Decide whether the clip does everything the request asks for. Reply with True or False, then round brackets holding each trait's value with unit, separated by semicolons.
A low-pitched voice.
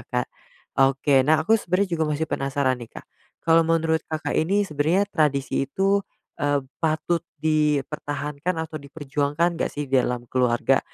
False (150 Hz)